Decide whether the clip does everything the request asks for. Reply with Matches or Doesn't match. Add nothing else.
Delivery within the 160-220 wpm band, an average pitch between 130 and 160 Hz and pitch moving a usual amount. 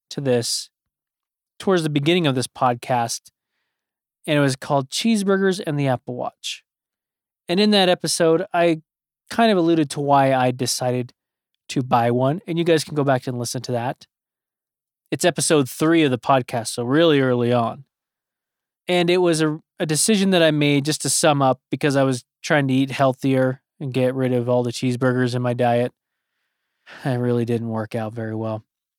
Matches